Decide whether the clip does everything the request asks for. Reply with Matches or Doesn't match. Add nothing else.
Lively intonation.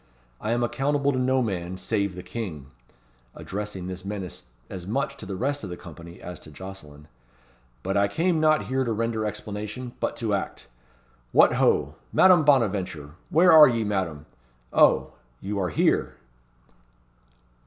Matches